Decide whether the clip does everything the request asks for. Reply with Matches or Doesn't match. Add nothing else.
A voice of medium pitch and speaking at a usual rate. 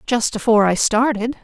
Doesn't match